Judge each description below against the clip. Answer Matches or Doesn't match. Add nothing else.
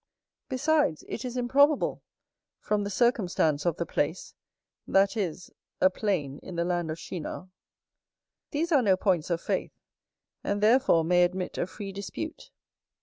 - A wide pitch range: Matches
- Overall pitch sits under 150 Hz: Doesn't match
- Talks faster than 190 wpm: Doesn't match